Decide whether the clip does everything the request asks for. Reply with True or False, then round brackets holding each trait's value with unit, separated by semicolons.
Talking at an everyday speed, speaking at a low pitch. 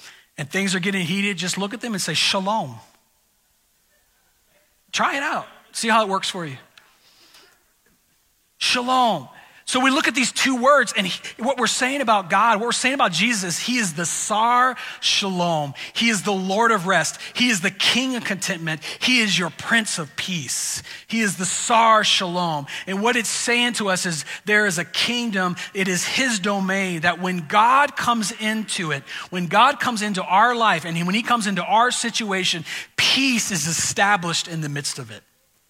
False (185 wpm; 200 Hz)